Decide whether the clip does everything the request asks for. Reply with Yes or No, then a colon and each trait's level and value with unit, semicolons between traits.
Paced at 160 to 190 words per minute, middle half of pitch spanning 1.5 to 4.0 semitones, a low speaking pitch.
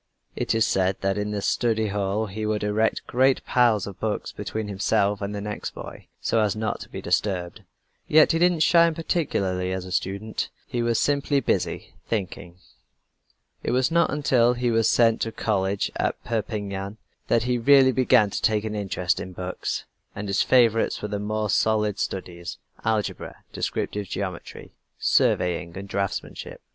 Yes: average, 170 wpm; average, 3.1 semitones; low, 105 Hz